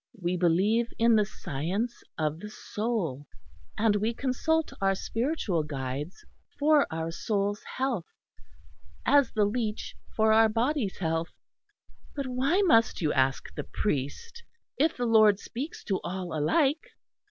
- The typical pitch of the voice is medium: No, high, 215 Hz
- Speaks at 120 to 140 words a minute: Yes, slow, 135 wpm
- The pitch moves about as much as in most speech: No, wide, 6.6 semitones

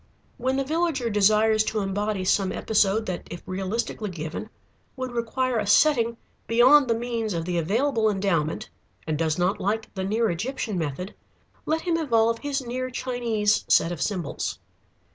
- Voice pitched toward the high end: Yes, high, 220 Hz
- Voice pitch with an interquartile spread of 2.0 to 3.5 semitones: No, average, 4.4 semitones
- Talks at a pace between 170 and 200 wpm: No, average, 160 wpm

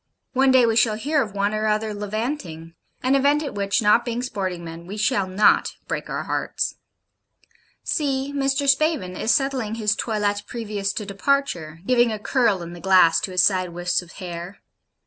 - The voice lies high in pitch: Yes, high, 215 Hz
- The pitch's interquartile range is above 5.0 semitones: Yes, wide, 5.5 semitones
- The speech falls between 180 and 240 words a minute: Yes, average, 185 wpm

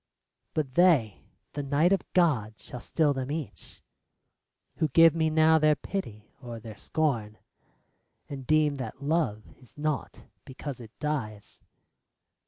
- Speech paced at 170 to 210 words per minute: No, average, 140 wpm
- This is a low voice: No, medium, 145 Hz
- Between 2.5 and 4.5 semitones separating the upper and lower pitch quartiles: No, average, 5.1 semitones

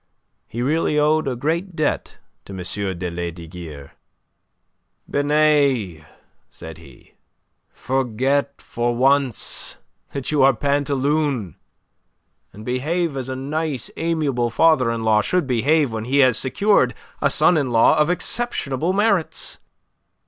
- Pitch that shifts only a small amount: No, average, 4.8 semitones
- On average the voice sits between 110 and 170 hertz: Yes, low, 135 Hz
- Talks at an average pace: No, slow, 125 wpm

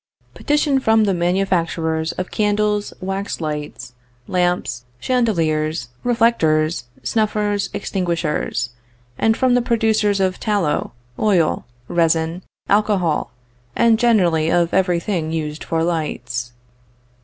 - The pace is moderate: No, slow, 105 wpm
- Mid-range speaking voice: Yes, medium, 180 Hz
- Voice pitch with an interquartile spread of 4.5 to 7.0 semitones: Yes, average, 4.8 semitones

